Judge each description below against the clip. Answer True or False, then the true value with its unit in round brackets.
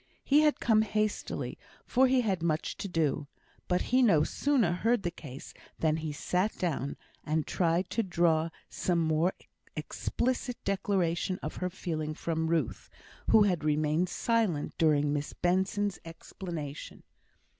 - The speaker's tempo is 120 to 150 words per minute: True (145 wpm)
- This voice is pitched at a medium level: True (175 Hz)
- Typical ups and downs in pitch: True (4.6 semitones)